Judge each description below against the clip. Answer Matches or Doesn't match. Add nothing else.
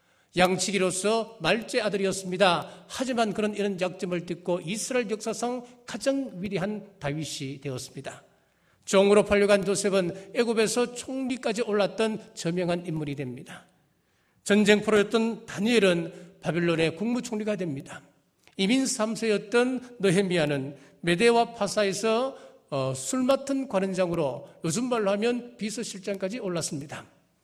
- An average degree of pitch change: Matches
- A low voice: Doesn't match